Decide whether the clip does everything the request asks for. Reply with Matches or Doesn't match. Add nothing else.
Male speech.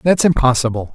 Matches